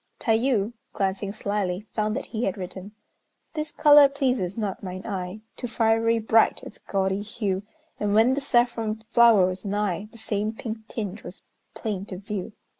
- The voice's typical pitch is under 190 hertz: No, high, 215 Hz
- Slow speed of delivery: No, average, 165 wpm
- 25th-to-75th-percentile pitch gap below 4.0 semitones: Yes, average, 2.8 semitones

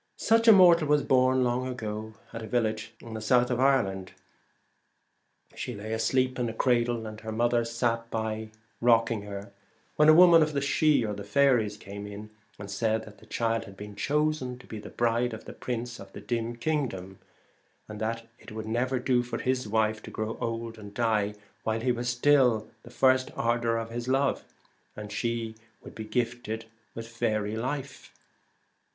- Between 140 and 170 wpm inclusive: No, average, 185 wpm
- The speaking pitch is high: No, low, 115 Hz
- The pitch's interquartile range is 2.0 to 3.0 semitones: Yes, narrow, 2.6 semitones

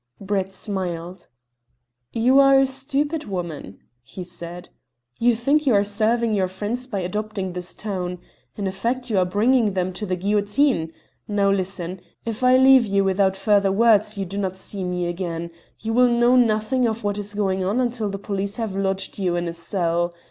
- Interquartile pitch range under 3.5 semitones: No, average, 3.8 semitones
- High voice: Yes, high, 200 Hz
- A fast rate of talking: No, average, 185 wpm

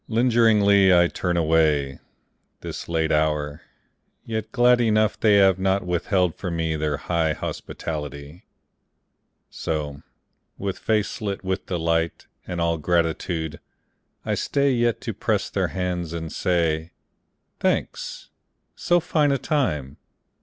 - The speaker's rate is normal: No, slow, 125 wpm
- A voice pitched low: Yes, very low, 85 Hz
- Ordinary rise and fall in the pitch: Yes, average, 4.6 semitones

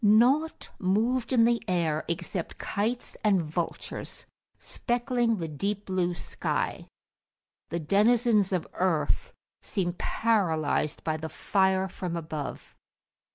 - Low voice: No, high, 190 Hz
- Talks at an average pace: No, slow, 110 wpm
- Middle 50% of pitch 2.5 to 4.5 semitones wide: No, average, 5.3 semitones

